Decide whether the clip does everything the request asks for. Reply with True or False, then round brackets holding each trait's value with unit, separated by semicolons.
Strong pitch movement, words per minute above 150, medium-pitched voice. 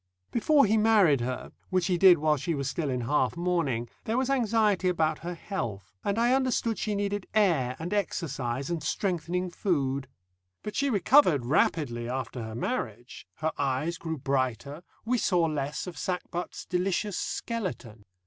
True (7.0 semitones; 160 wpm; 170 Hz)